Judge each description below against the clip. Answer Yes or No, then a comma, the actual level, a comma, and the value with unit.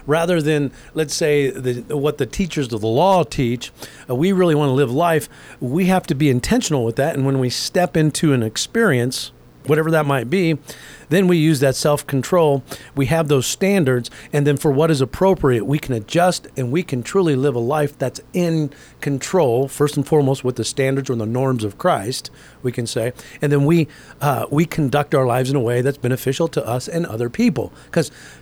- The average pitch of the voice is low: No, medium, 145 Hz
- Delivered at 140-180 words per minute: No, fast, 205 wpm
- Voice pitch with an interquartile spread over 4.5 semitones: No, average, 3.9 semitones